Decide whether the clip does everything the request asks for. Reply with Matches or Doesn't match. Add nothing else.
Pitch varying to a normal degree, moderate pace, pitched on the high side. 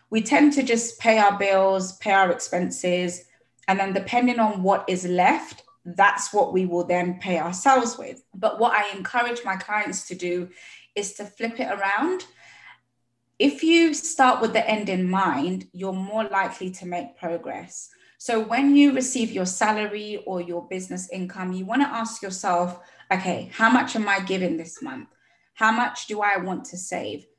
Matches